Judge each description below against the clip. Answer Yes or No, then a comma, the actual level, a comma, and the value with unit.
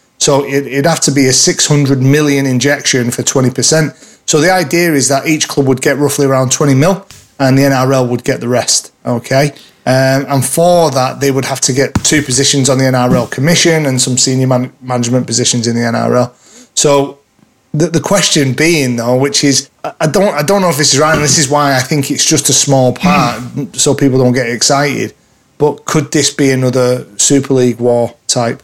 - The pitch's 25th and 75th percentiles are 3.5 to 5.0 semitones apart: No, average, 2.7 semitones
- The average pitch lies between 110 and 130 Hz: No, medium, 140 Hz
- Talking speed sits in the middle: No, fast, 210 wpm